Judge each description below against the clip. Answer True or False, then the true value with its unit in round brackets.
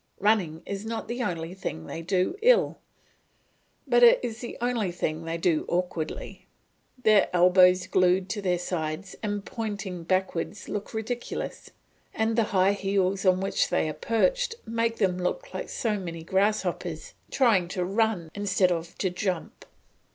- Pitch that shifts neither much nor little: True (3.8 semitones)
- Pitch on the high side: True (195 Hz)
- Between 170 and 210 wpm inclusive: False (155 wpm)